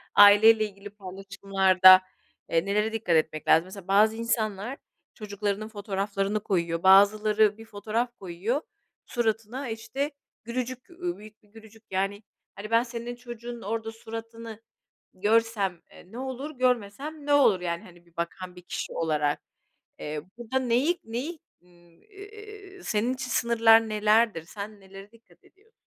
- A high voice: Yes, high, 215 Hz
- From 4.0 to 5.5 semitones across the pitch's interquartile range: No, average, 3.3 semitones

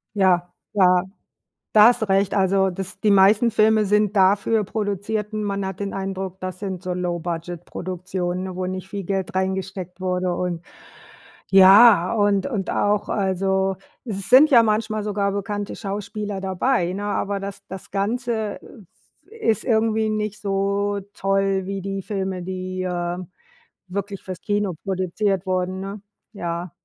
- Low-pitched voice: No, high, 195 Hz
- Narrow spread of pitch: Yes, narrow, 1.9 semitones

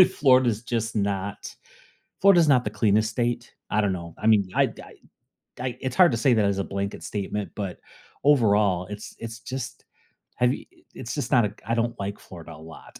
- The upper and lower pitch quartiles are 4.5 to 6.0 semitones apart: No, average, 3.3 semitones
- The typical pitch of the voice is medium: No, low, 110 Hz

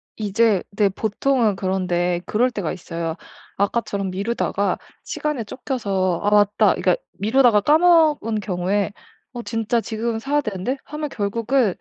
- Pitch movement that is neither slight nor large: Yes, average, 4.0 semitones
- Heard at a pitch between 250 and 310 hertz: No, high, 210 Hz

